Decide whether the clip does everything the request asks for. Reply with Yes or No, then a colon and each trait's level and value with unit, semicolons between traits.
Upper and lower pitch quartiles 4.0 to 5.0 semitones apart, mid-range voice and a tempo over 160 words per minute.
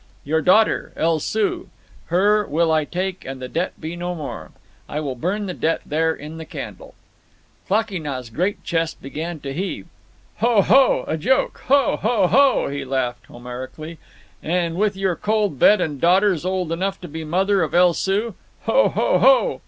Yes: average, 4.4 semitones; medium, 175 Hz; average, 175 wpm